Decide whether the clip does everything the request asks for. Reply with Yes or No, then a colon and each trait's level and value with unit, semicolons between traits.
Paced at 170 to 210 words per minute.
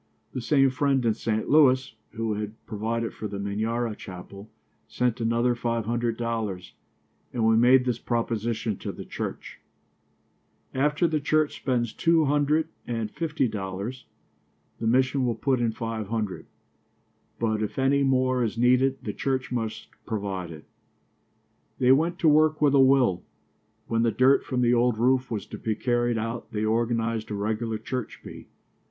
No: average, 160 wpm